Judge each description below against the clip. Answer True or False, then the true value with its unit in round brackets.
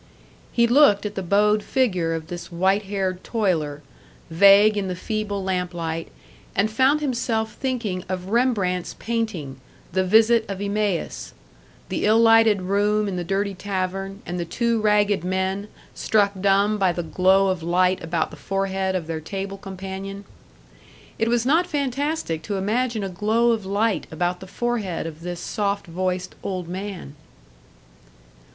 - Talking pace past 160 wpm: False (155 wpm)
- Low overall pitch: False (195 Hz)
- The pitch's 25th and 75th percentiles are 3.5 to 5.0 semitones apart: False (2.9 semitones)